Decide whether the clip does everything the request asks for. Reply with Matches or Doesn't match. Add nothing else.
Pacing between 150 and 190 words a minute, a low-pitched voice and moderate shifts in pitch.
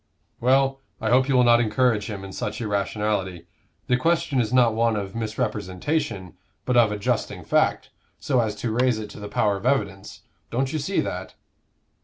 Matches